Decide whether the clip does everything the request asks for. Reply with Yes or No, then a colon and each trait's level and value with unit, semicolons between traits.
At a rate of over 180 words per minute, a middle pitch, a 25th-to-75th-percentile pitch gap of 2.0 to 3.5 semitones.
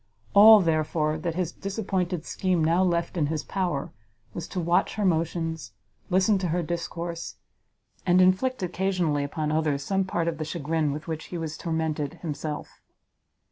No: average, 160 wpm; medium, 170 Hz; average, 2.8 semitones